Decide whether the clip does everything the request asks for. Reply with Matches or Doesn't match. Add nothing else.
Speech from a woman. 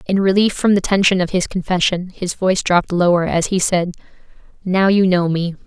Matches